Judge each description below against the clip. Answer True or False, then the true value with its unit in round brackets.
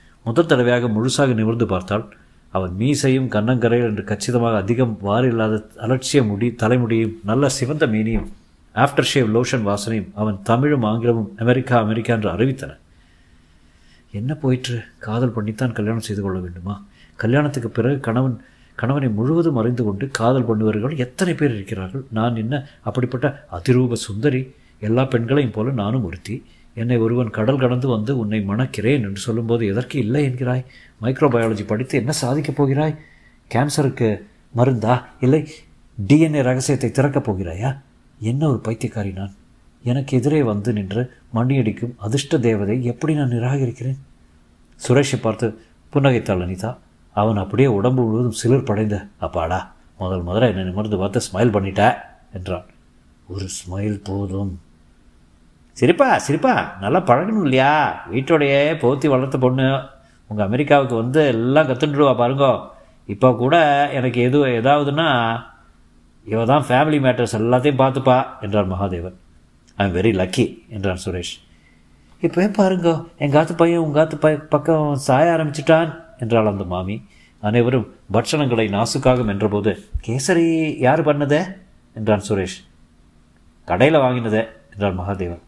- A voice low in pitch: True (120 Hz)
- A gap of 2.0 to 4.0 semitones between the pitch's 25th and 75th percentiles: False (4.7 semitones)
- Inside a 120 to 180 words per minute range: True (125 wpm)